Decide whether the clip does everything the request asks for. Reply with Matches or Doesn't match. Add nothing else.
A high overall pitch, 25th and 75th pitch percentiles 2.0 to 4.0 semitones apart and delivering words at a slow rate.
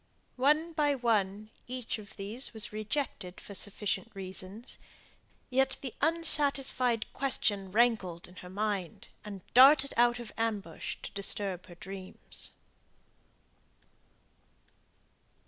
Doesn't match